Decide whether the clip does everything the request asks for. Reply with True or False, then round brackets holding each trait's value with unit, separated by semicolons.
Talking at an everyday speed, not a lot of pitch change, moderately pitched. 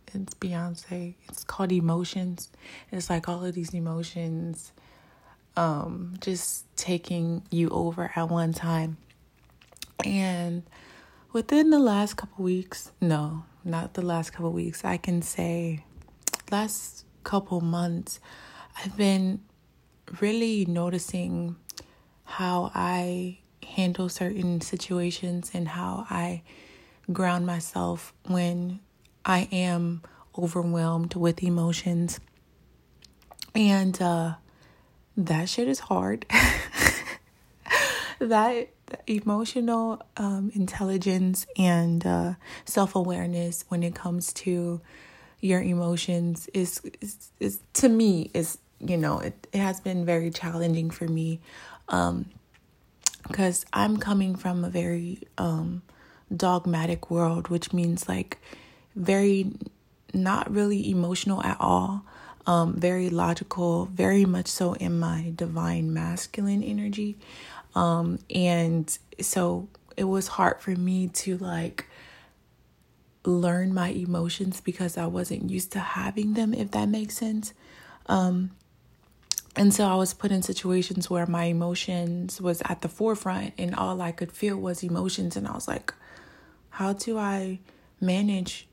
False (120 wpm; 2.1 semitones; 180 Hz)